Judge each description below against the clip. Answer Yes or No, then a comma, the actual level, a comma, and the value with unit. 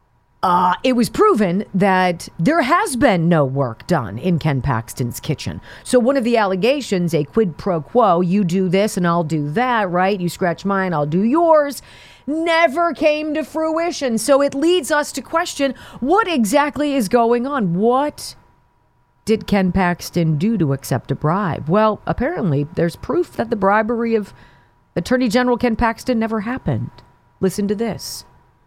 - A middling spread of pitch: No, wide, 8.3 semitones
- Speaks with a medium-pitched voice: No, high, 200 Hz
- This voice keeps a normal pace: Yes, average, 165 wpm